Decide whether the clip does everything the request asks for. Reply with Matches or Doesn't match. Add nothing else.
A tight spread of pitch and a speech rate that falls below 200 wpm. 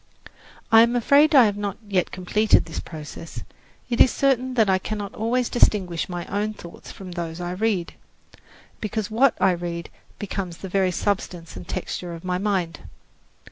Doesn't match